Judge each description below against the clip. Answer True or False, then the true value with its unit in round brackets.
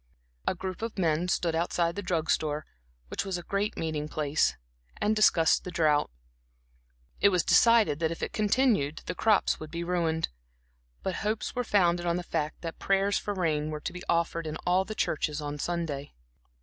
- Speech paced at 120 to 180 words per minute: False (190 wpm)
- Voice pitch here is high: False (170 Hz)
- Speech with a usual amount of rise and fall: True (3.8 semitones)